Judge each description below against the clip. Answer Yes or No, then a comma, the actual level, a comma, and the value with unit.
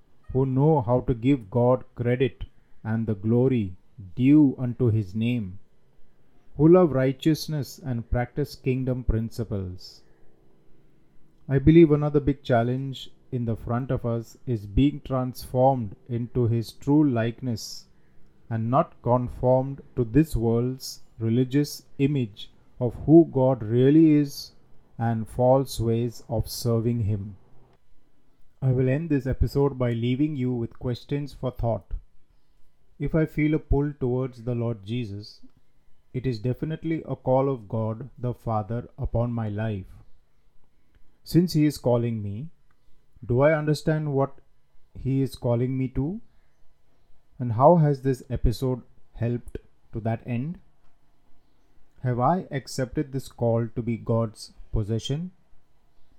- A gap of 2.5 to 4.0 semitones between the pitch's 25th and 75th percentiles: Yes, average, 3.3 semitones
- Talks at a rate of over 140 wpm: No, average, 130 wpm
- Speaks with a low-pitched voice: Yes, low, 125 Hz